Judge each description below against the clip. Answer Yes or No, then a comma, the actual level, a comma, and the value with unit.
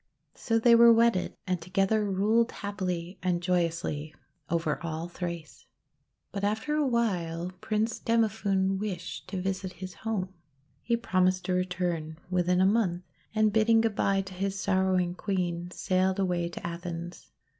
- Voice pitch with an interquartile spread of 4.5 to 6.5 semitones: No, average, 3.2 semitones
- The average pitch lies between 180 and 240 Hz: Yes, medium, 185 Hz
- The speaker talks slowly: No, average, 150 wpm